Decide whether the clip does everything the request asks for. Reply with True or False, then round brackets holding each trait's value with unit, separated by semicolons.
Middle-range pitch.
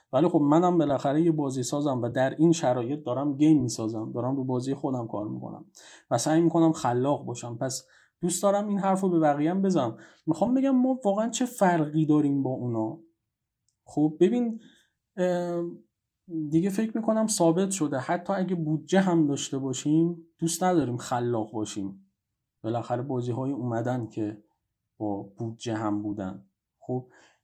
True (145 Hz)